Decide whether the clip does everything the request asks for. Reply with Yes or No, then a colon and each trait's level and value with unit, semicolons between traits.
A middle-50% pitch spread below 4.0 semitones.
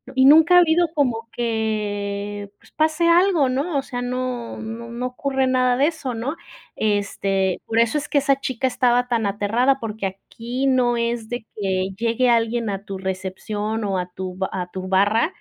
No: average, 4.3 semitones